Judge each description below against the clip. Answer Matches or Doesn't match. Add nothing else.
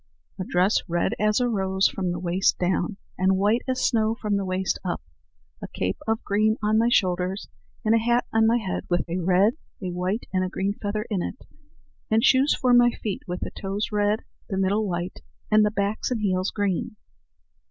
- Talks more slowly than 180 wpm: Doesn't match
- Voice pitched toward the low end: Doesn't match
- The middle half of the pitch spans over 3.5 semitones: Doesn't match